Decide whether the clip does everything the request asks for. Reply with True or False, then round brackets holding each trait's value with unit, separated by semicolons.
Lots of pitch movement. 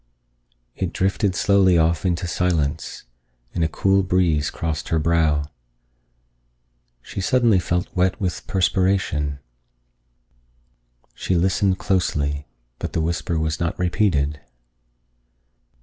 False (3.1 semitones)